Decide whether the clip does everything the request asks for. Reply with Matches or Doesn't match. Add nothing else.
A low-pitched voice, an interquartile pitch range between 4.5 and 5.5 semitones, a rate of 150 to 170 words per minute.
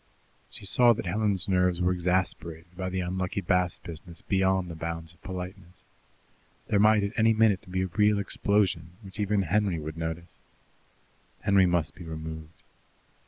Doesn't match